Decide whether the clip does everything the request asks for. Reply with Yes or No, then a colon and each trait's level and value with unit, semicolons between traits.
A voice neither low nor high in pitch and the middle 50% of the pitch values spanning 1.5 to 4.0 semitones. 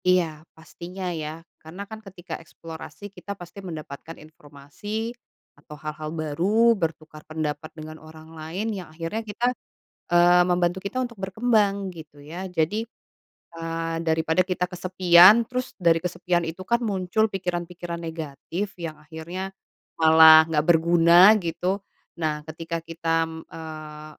Yes: medium, 170 Hz; average, 3.0 semitones